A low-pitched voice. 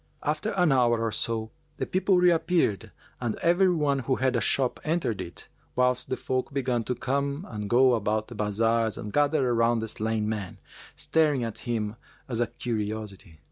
Yes: low, 120 Hz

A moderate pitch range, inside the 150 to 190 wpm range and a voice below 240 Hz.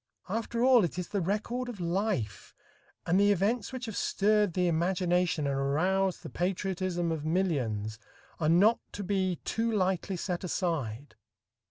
Yes: average, 3.5 semitones; average, 155 wpm; medium, 185 Hz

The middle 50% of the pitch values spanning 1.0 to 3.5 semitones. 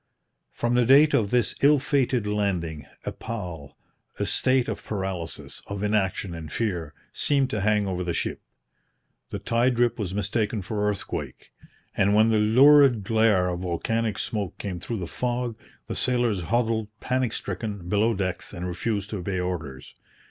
No: average, 4.4 semitones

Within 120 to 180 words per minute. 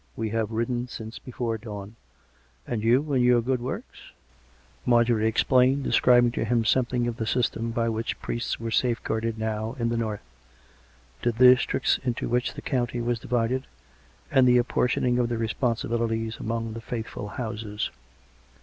Yes: average, 165 wpm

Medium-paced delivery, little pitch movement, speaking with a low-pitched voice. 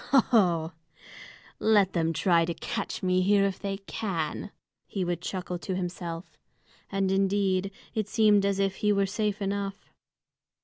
No: average, 150 wpm; narrow, 2.2 semitones; high, 195 Hz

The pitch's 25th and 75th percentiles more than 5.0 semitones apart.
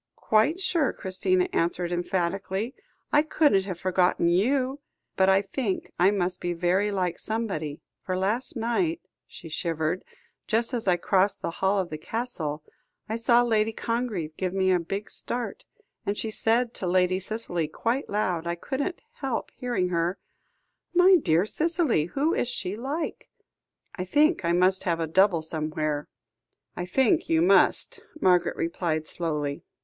Yes: wide, 5.4 semitones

